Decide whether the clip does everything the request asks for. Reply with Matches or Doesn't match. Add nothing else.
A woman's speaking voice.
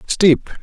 Doesn't match